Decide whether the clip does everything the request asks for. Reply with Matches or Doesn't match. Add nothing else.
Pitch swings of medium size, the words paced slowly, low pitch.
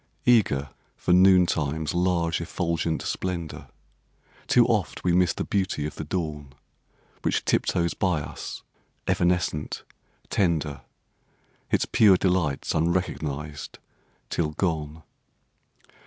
Matches